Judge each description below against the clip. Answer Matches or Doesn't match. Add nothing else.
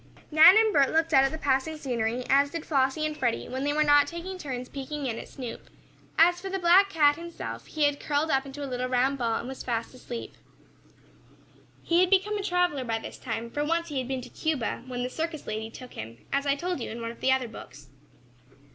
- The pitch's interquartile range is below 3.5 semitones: Doesn't match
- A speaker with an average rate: Doesn't match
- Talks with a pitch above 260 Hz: Matches